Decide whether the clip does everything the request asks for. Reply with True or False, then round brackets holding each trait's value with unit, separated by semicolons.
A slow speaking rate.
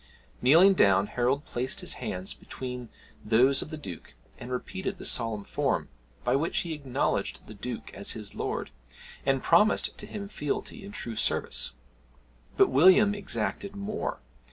False (155 wpm)